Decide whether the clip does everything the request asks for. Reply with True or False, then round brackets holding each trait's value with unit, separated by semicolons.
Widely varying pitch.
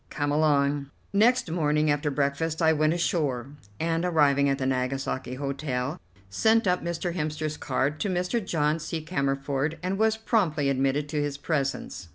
False (3.2 semitones)